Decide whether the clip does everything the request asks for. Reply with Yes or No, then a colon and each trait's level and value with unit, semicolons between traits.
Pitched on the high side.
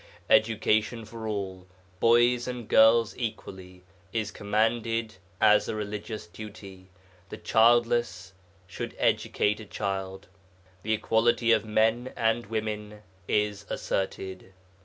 No: low, 110 Hz